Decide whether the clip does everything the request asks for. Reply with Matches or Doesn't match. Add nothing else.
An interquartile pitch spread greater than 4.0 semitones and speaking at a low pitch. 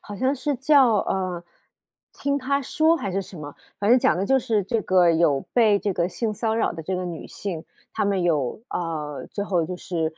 Doesn't match